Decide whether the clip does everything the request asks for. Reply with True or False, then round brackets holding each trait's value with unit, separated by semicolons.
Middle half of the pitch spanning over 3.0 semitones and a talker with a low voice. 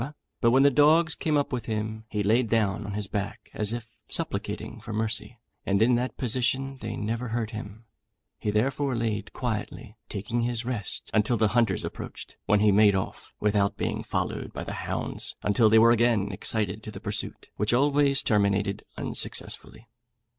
False (2.7 semitones; 110 Hz)